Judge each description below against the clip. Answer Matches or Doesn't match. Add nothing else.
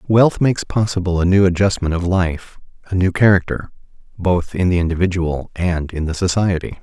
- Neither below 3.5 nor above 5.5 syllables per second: Matches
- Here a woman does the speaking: Doesn't match